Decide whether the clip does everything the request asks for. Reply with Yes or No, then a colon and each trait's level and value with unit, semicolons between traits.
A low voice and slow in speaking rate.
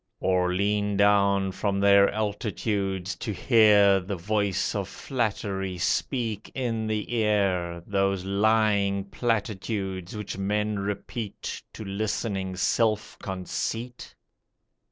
Yes: low, 100 Hz; slow, 105 wpm